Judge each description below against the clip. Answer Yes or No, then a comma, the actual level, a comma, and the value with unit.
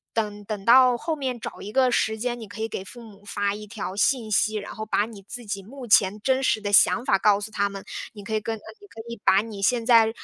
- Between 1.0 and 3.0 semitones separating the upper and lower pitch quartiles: Yes, average, 2.7 semitones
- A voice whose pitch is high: Yes, high, 220 Hz